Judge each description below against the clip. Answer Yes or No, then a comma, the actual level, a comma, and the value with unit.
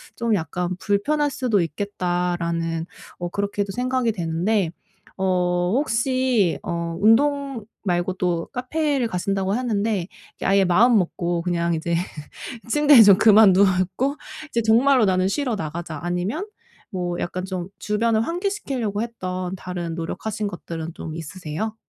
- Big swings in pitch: No, average, 4.8 semitones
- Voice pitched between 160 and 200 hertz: Yes, high, 195 Hz